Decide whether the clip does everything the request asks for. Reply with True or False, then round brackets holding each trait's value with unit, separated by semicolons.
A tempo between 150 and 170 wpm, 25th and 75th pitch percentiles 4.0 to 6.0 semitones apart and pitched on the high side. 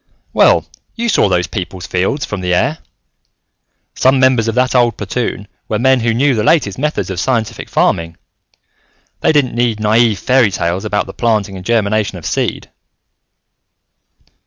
False (160 wpm; 4.7 semitones; 115 Hz)